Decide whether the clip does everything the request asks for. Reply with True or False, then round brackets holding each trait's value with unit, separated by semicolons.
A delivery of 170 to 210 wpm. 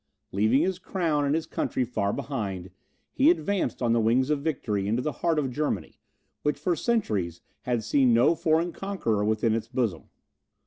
True (175 wpm)